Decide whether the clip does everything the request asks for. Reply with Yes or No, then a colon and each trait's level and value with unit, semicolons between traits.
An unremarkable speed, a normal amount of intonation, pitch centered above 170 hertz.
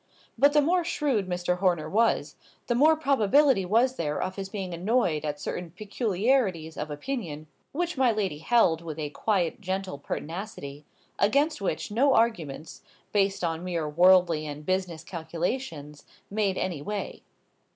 No: average, 150 wpm; wide, 6.3 semitones; medium, 185 Hz